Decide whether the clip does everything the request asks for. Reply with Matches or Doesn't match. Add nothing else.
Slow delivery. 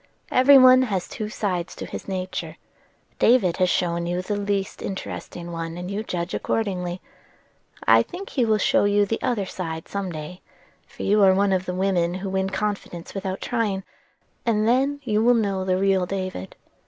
Doesn't match